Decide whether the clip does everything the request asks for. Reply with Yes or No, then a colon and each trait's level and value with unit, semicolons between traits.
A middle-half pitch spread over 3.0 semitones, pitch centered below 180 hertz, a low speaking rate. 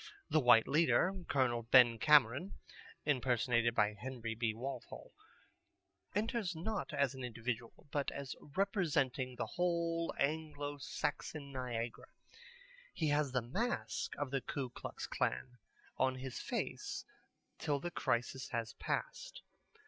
Yes: average, 4.1 semitones; low, 135 Hz; slow, 125 wpm